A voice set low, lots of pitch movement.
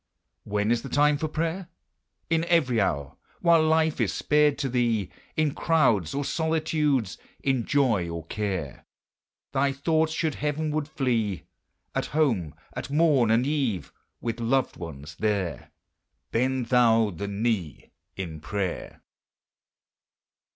Yes: low, 125 Hz; wide, 6.8 semitones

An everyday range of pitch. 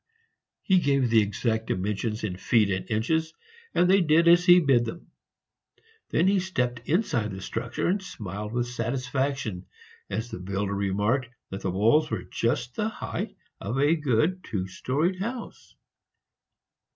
No: wide, 7.5 semitones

